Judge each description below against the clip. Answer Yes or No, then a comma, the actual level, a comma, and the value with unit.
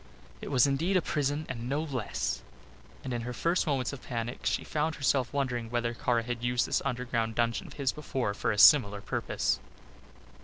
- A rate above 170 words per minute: Yes, average, 190 wpm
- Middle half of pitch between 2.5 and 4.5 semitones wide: Yes, average, 3.2 semitones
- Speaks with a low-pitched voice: Yes, low, 125 Hz